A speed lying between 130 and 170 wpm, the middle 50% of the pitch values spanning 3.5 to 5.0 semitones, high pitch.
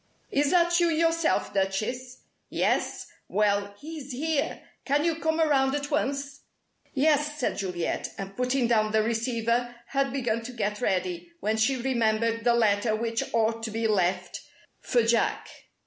Yes: average, 150 wpm; average, 4.6 semitones; high, 235 Hz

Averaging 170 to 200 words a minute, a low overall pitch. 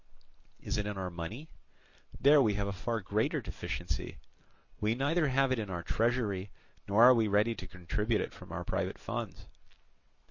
Yes: average, 175 wpm; low, 110 Hz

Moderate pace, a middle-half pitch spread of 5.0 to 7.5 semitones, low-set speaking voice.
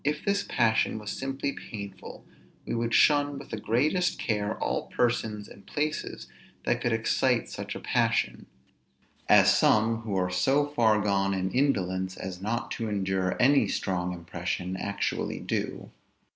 Yes: average, 150 wpm; wide, 5.4 semitones; low, 110 Hz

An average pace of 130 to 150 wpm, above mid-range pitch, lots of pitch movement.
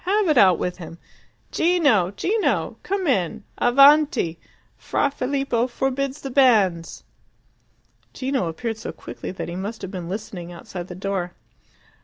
Yes: average, 140 wpm; high, 225 Hz; wide, 7.2 semitones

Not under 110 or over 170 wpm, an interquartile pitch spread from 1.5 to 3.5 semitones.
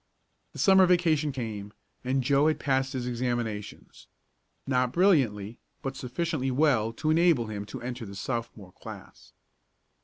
No: average, 140 wpm; average, 5.0 semitones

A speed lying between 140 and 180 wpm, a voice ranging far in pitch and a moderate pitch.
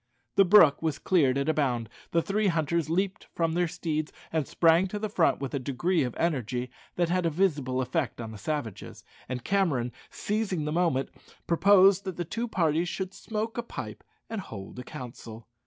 No: average, 190 wpm; wide, 6.0 semitones; medium, 165 Hz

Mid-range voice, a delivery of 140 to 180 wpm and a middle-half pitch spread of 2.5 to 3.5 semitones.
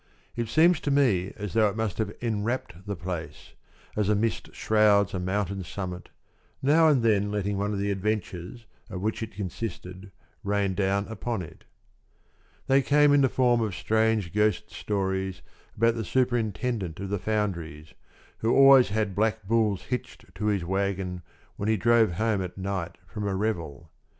No: low, 105 Hz; average, 170 wpm; average, 2.9 semitones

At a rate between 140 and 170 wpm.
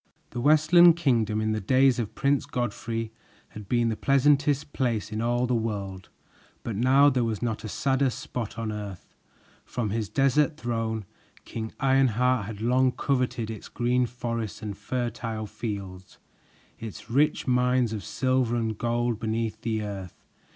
Yes: average, 155 wpm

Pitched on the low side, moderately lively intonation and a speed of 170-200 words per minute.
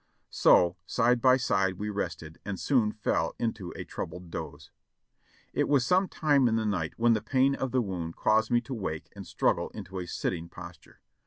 No: low, 105 Hz; wide, 5.7 semitones; average, 190 wpm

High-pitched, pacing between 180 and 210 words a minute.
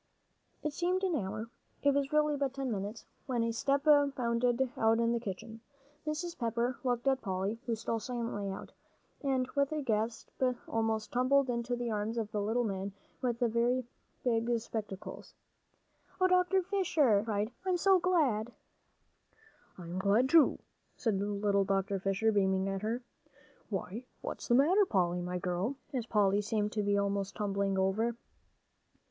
No: high, 230 Hz; average, 160 wpm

